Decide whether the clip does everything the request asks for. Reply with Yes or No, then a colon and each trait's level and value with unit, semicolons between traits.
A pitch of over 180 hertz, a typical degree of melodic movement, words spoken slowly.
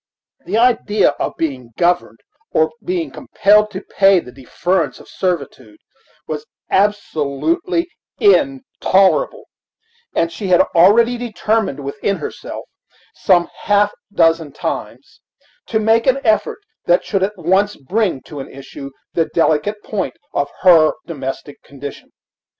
No: high, 190 Hz; wide, 5.9 semitones; slow, 125 wpm